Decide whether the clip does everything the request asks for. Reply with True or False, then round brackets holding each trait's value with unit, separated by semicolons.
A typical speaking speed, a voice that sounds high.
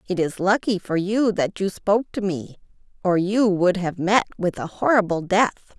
True (195 wpm; 195 Hz)